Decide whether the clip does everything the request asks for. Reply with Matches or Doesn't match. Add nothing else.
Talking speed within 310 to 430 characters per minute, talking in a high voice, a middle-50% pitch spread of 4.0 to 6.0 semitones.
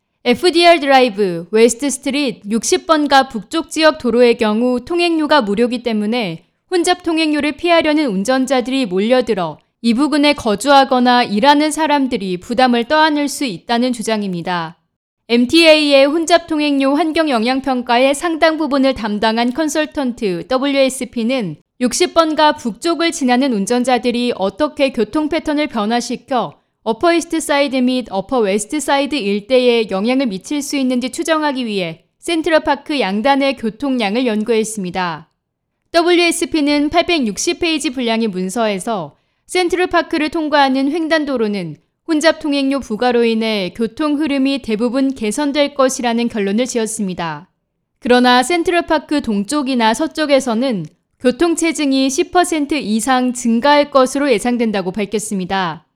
Matches